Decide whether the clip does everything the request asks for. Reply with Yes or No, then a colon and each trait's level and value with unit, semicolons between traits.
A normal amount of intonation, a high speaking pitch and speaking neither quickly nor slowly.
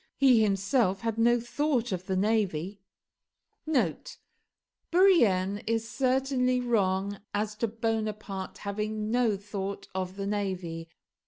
No: average, 3.5 semitones; high, 210 Hz; slow, 110 wpm